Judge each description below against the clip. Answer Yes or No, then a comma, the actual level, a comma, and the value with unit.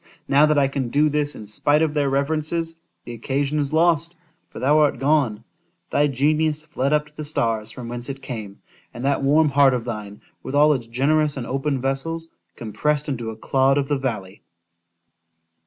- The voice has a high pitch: No, medium, 140 Hz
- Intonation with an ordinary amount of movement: Yes, average, 3.3 semitones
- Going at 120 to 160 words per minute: No, average, 175 wpm